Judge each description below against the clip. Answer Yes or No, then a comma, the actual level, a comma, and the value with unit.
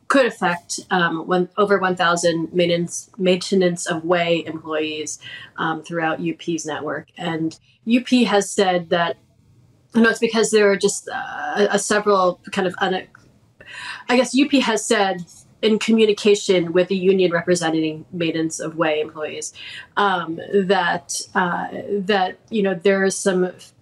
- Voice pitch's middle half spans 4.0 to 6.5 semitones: No, average, 3.6 semitones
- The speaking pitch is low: No, medium, 185 Hz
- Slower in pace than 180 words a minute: Yes, average, 150 wpm